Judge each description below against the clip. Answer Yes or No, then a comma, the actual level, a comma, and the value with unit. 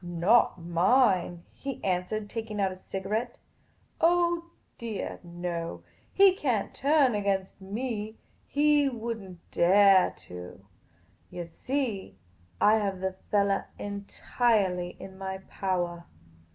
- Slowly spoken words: Yes, slow, 120 wpm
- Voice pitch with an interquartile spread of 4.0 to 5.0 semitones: Yes, average, 4.7 semitones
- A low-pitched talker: No, high, 200 Hz